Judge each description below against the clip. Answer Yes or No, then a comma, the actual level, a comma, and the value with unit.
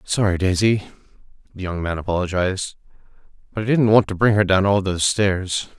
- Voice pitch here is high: No, very low, 95 Hz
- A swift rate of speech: No, average, 175 wpm